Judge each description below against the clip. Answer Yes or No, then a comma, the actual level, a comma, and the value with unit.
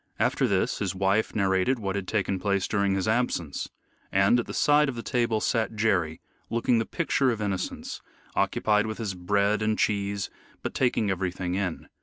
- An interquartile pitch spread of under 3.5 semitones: Yes, average, 2.9 semitones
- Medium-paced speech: Yes, average, 180 wpm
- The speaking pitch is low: Yes, low, 100 Hz